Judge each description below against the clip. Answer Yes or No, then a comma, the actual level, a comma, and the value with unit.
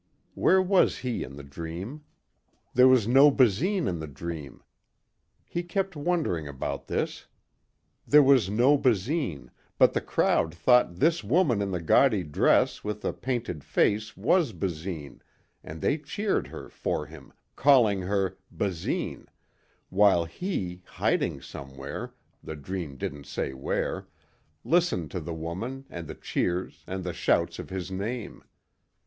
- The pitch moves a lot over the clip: Yes, wide, 8.2 semitones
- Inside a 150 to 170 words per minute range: No, average, 140 wpm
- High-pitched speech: No, low, 100 Hz